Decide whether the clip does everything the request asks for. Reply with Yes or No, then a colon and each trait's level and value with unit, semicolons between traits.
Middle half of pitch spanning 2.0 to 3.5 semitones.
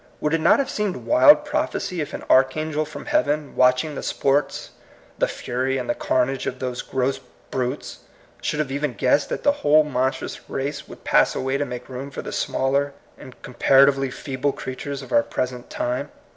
Yes: narrow, 2.6 semitones